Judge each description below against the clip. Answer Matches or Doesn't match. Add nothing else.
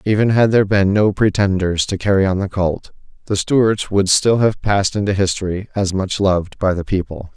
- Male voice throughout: Matches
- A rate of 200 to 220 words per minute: Matches